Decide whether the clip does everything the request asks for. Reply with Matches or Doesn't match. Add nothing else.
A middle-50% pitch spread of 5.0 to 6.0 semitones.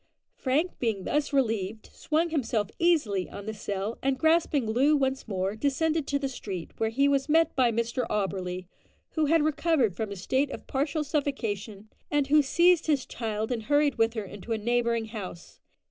Matches